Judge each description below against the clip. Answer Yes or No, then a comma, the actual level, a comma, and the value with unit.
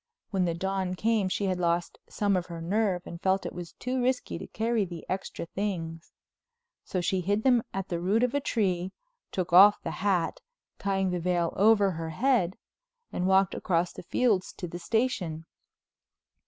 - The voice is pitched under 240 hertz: Yes, high, 190 Hz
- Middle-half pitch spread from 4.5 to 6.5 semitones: No, average, 3.1 semitones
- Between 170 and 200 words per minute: Yes, average, 180 wpm